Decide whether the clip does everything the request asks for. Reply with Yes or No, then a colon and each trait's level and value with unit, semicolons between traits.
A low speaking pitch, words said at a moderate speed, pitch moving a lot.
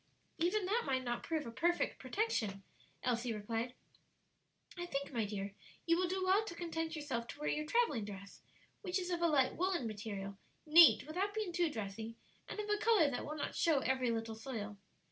No: very high, 290 Hz; average, 195 wpm; wide, 7.6 semitones